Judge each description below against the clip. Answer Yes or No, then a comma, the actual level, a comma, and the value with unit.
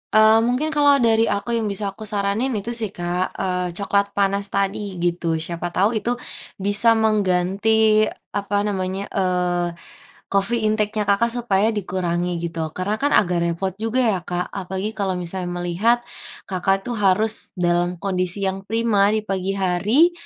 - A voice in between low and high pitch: No, high, 200 Hz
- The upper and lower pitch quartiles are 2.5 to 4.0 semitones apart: Yes, average, 3.1 semitones